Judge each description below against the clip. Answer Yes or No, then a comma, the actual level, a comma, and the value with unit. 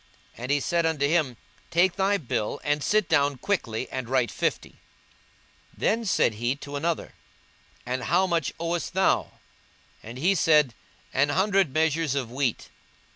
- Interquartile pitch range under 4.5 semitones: No, average, 4.9 semitones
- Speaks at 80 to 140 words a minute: No, average, 155 wpm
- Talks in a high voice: No, medium, 150 Hz